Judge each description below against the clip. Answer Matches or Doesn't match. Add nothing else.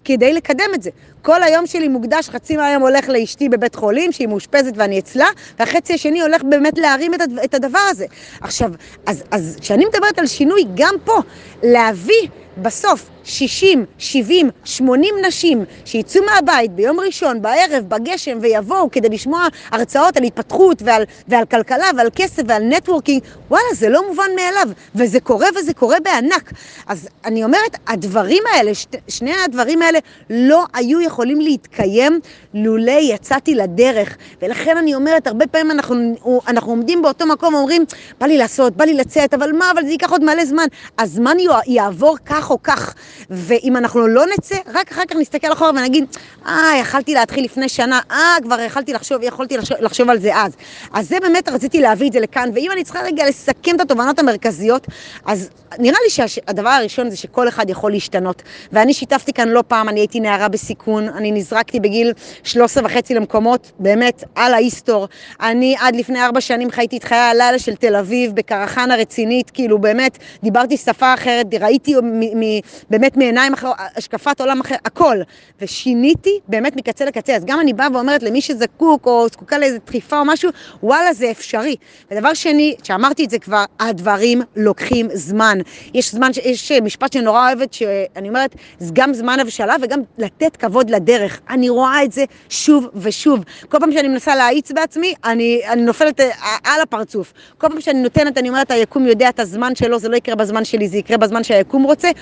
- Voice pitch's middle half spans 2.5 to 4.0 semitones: Doesn't match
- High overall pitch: Matches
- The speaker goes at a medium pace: Doesn't match